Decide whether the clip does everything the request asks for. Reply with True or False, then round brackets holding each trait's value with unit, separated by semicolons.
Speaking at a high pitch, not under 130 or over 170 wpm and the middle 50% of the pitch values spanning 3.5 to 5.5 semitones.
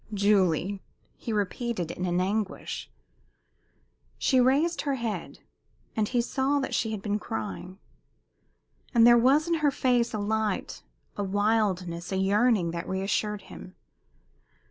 True (210 Hz; 135 wpm; 4.2 semitones)